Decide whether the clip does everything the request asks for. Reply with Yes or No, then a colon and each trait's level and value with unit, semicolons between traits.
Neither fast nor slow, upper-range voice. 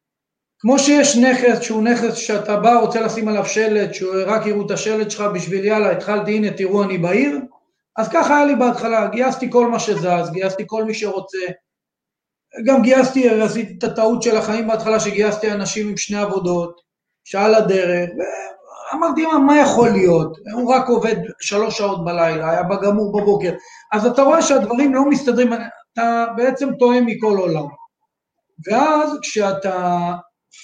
No: fast, 155 wpm; high, 220 Hz